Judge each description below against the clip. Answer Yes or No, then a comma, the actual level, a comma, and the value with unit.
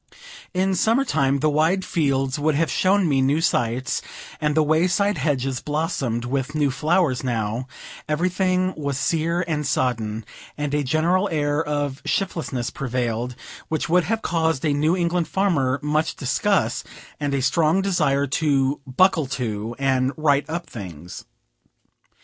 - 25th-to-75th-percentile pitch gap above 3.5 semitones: Yes, average, 4.1 semitones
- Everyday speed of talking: Yes, average, 150 wpm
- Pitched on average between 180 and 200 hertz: No, medium, 150 Hz